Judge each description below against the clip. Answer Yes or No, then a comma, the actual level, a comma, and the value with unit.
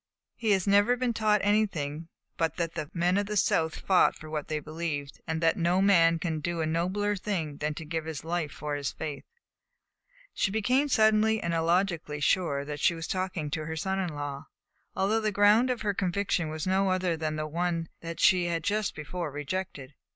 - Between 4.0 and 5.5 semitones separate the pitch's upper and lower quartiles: Yes, average, 4.3 semitones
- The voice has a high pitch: No, medium, 170 Hz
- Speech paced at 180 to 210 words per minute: Yes, average, 200 wpm